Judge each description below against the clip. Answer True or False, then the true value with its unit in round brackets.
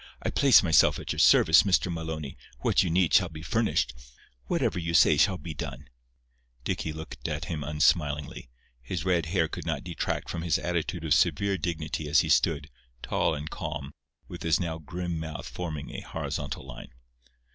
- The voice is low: True (80 Hz)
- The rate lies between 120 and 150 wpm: False (180 wpm)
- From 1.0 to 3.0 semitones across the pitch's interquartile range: True (2.6 semitones)